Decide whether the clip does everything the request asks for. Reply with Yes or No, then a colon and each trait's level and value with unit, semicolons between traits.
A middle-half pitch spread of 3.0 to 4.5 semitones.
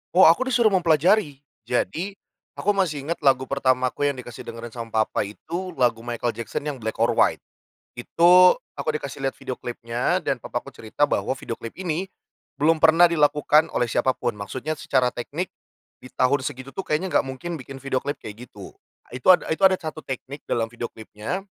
No: wide, 5.4 semitones